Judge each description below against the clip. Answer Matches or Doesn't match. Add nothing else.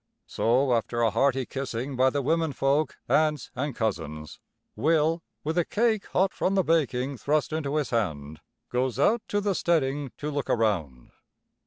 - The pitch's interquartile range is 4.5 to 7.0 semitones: Matches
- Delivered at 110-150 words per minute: Doesn't match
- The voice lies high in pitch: Doesn't match